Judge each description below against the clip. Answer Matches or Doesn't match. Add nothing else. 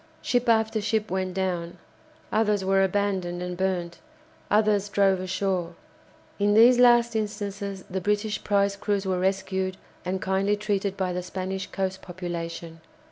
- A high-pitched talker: Matches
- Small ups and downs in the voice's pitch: Matches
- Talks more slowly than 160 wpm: Matches